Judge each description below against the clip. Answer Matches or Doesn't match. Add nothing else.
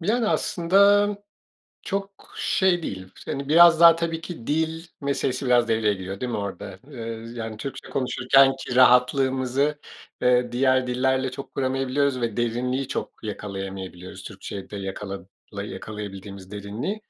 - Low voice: Matches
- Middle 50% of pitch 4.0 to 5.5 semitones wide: Matches